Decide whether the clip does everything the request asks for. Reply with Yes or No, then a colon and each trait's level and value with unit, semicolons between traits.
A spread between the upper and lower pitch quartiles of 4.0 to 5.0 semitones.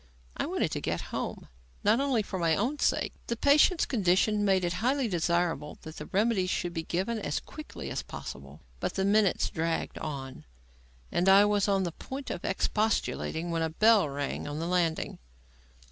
Yes: average, 4.6 semitones